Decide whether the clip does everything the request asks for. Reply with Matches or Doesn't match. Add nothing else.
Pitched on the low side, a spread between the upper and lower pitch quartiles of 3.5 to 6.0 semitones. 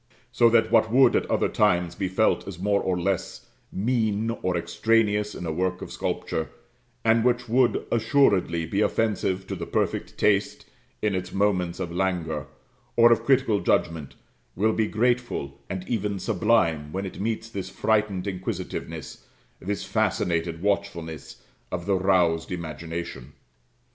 Matches